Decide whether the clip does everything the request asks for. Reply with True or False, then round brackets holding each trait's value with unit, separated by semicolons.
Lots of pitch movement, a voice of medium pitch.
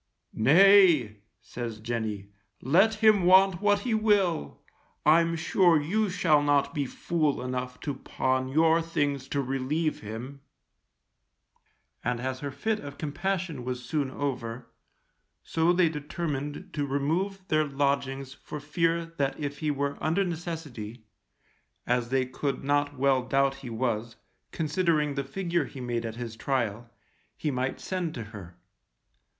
False (4.6 semitones; 145 Hz)